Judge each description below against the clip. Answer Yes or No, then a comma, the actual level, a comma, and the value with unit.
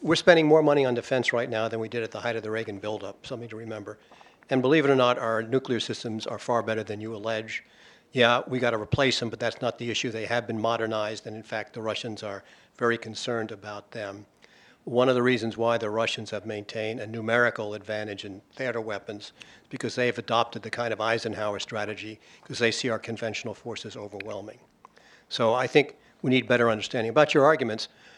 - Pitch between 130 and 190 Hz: No, low, 115 Hz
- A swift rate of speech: Yes, fast, 215 wpm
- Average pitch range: No, narrow, 1.9 semitones